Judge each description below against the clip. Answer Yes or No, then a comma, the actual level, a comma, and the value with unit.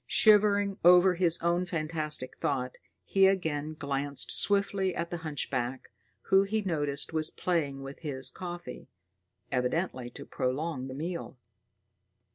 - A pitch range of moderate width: Yes, average, 4.7 semitones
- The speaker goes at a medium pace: No, slow, 125 wpm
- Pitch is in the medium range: Yes, medium, 160 Hz